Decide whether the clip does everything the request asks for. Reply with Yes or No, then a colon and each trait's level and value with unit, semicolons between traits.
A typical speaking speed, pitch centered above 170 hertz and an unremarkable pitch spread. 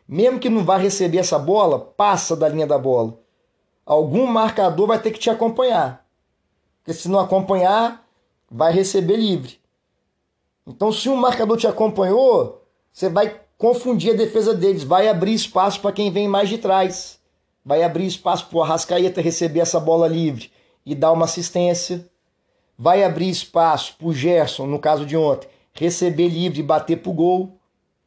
Yes: average, 165 wpm; medium, 185 Hz; average, 4.3 semitones